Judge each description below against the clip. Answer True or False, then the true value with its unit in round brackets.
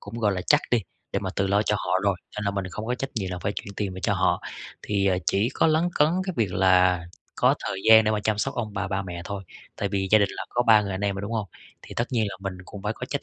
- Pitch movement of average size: False (2.3 semitones)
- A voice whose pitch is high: False (100 Hz)